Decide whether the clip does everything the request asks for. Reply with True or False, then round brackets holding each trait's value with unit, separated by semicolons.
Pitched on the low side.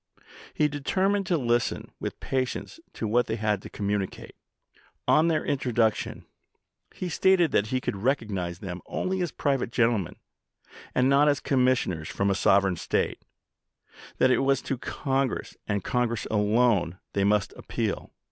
True (120 Hz)